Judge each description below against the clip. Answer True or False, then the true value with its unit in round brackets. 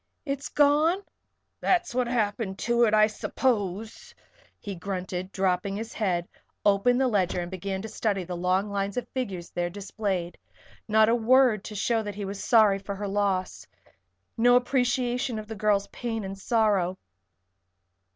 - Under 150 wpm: False (160 wpm)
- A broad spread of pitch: False (3.7 semitones)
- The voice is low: False (210 Hz)